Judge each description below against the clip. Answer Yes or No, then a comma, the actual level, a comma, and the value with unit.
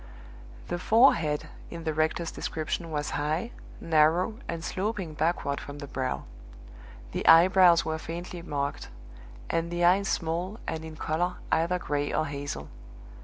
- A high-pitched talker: No, medium, 165 Hz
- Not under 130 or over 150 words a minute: Yes, average, 140 wpm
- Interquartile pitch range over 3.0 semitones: No, narrow, 2.6 semitones